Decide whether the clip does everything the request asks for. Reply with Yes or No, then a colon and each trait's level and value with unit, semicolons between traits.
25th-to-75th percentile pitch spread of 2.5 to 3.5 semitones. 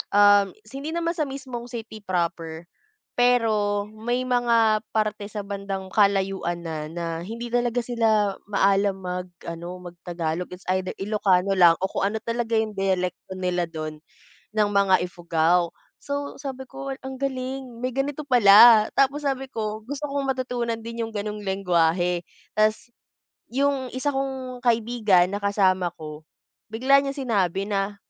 No: average, 4.8 semitones